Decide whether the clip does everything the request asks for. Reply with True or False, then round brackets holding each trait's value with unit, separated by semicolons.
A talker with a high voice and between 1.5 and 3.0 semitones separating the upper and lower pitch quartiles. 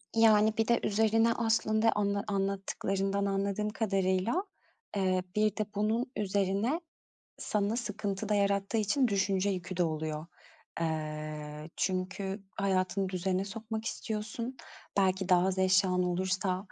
True (195 Hz; 2.5 semitones)